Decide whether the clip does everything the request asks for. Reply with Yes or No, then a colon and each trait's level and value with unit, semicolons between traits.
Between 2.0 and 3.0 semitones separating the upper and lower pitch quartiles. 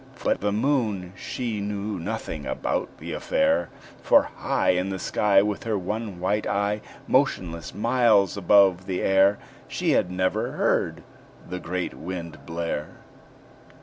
Yes: narrow, 2.5 semitones